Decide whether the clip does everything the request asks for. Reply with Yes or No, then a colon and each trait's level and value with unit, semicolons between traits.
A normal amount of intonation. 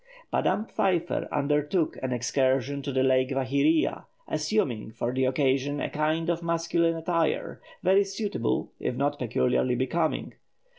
Yes: average, 4.1 semitones